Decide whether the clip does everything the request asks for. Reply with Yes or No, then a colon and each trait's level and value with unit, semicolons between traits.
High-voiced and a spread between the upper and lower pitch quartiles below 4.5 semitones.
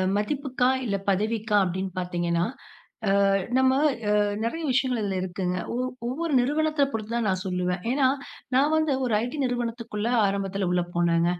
No: high, 215 Hz; wide, 5.5 semitones